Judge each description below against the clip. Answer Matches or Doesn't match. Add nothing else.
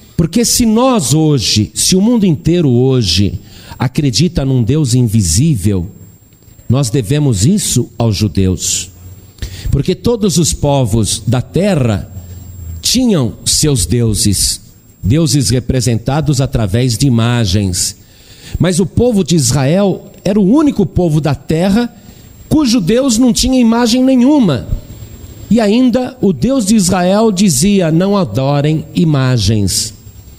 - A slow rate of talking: Matches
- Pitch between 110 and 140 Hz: Matches